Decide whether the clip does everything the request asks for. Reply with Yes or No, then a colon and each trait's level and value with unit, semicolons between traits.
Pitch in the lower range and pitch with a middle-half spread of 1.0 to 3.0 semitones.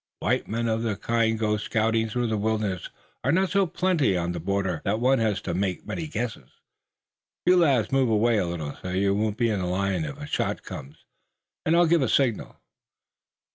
No: low, 110 Hz; average, 4.1 semitones